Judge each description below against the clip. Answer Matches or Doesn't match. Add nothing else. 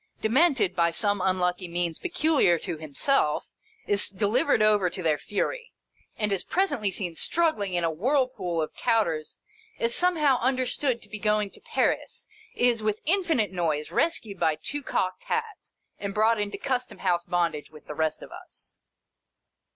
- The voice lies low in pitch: Doesn't match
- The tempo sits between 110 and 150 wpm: Doesn't match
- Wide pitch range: Matches